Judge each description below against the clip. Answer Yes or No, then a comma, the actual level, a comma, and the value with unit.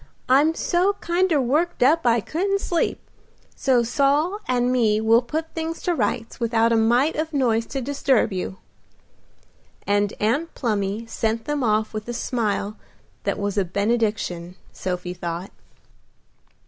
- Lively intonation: Yes, wide, 5.7 semitones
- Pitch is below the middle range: No, high, 235 Hz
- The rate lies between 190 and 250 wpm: No, average, 145 wpm